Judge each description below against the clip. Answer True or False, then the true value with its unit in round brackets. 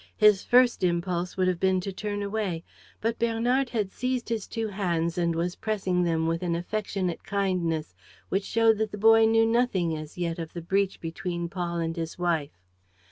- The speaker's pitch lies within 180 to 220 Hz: True (185 Hz)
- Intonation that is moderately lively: True (4.2 semitones)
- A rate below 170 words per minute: False (190 wpm)